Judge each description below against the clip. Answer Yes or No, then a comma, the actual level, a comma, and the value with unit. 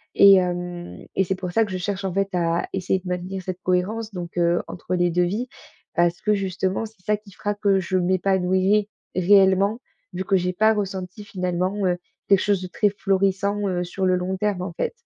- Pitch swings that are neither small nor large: No, narrow, 1.8 semitones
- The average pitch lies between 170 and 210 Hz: Yes, high, 190 Hz